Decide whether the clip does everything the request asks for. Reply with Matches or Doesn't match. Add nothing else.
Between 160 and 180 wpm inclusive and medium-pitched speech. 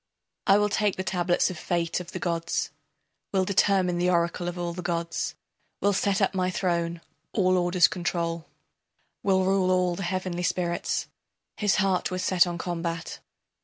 Matches